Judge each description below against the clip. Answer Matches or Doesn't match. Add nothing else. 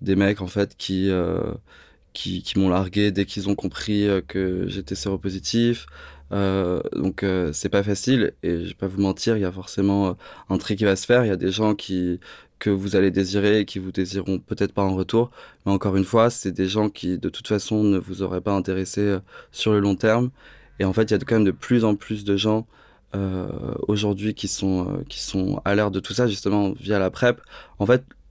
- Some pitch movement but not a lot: Doesn't match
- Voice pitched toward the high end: Doesn't match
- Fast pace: Matches